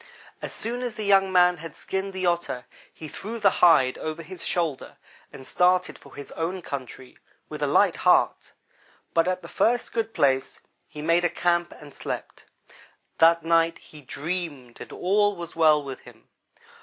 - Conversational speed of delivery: Yes, average, 175 wpm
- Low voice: No, medium, 170 Hz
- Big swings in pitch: No, average, 3.7 semitones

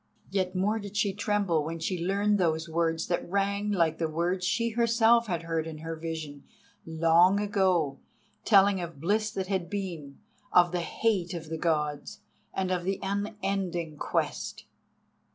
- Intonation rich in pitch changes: No, average, 3.7 semitones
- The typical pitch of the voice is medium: Yes, medium, 180 Hz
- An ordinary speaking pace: Yes, average, 155 wpm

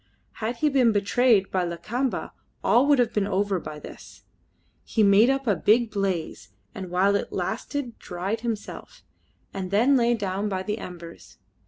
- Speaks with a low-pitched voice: No, high, 210 Hz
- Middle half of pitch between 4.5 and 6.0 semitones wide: No, average, 4.1 semitones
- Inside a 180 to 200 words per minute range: No, average, 165 wpm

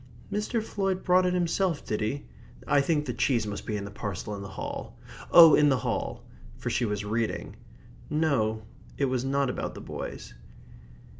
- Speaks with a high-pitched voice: No, low, 135 Hz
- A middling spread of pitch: No, wide, 7.4 semitones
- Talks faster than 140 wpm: Yes, average, 190 wpm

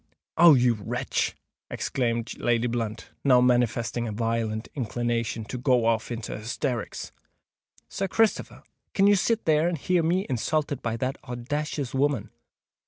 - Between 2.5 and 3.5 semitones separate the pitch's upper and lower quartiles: No, average, 4.2 semitones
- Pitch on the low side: Yes, low, 125 Hz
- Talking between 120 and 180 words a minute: Yes, average, 140 wpm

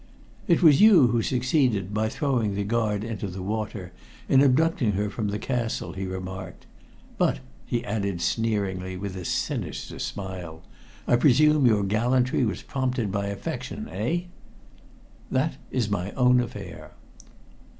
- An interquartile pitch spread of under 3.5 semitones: No, average, 4.3 semitones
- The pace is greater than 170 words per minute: No, average, 140 wpm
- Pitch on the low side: Yes, low, 110 Hz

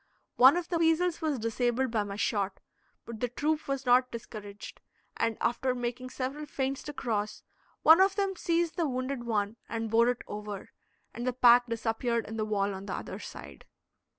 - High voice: Yes, high, 245 Hz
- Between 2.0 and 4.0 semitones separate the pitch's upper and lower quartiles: Yes, average, 3.7 semitones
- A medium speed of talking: Yes, average, 185 wpm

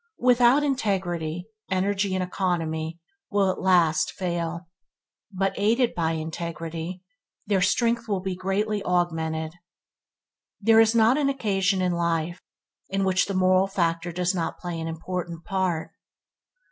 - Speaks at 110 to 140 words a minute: Yes, slow, 135 wpm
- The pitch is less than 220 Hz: Yes, medium, 185 Hz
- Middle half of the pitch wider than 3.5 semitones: No, average, 3.0 semitones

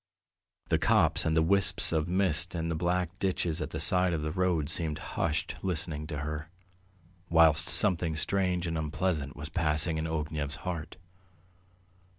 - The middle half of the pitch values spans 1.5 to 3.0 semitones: Yes, narrow, 2.6 semitones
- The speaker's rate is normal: Yes, average, 160 wpm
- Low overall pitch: Yes, very low, 80 Hz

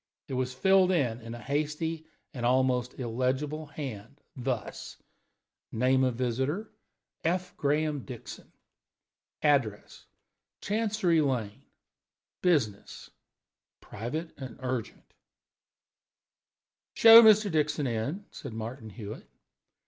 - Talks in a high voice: No, low, 135 Hz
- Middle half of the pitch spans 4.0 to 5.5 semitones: Yes, average, 4.9 semitones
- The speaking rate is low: Yes, slow, 95 wpm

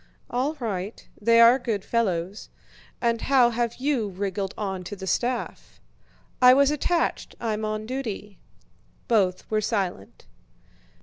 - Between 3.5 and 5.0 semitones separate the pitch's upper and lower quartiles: Yes, average, 3.8 semitones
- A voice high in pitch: Yes, high, 220 Hz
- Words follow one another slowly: Yes, slow, 125 wpm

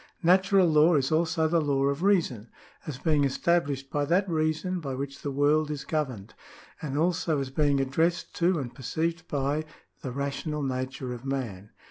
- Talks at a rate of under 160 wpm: No, average, 170 wpm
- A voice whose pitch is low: No, medium, 150 Hz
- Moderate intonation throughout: Yes, average, 3.2 semitones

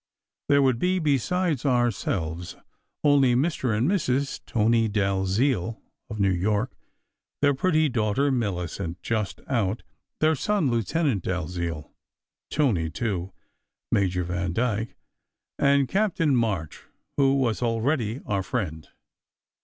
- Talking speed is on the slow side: Yes, slow, 110 wpm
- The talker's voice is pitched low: Yes, low, 115 Hz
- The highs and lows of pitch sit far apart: Yes, wide, 6.4 semitones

